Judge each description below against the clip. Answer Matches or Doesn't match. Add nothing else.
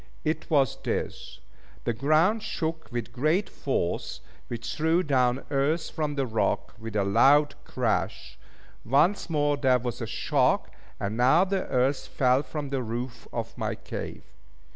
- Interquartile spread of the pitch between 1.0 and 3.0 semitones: Doesn't match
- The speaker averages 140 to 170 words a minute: Matches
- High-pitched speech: Doesn't match